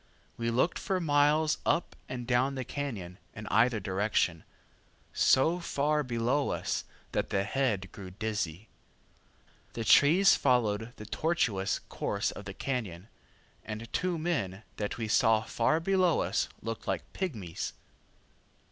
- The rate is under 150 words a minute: Yes, slow, 135 wpm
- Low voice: Yes, low, 120 Hz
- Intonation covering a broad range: Yes, wide, 5.9 semitones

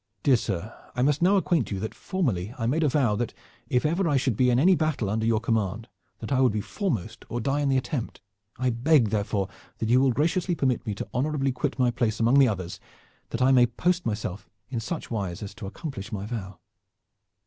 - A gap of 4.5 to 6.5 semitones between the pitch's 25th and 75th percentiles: Yes, average, 4.8 semitones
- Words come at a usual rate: No, fast, 220 wpm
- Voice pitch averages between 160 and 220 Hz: No, low, 125 Hz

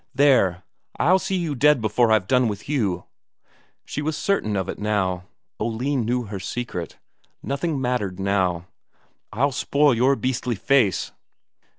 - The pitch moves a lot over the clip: Yes, wide, 5.9 semitones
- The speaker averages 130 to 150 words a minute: Yes, average, 145 wpm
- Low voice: Yes, low, 120 Hz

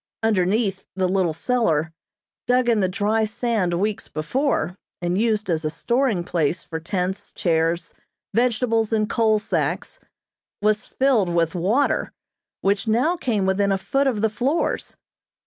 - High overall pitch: Yes, high, 205 Hz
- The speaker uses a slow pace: No, average, 145 wpm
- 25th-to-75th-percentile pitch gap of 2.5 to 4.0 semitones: No, average, 4.6 semitones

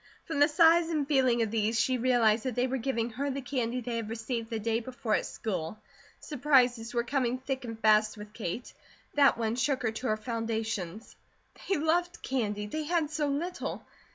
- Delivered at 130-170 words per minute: No, average, 195 wpm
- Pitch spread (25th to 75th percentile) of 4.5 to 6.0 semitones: No, average, 3.9 semitones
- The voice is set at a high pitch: Yes, high, 245 Hz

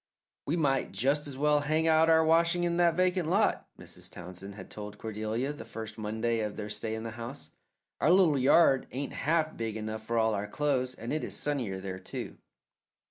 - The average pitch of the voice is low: Yes, low, 130 Hz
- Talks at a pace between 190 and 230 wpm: Yes, average, 200 wpm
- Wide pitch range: Yes, wide, 6.3 semitones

